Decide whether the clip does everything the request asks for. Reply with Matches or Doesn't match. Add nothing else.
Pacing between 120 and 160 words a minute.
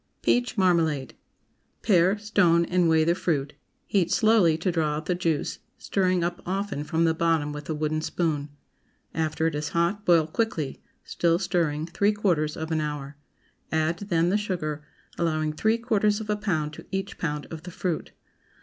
Doesn't match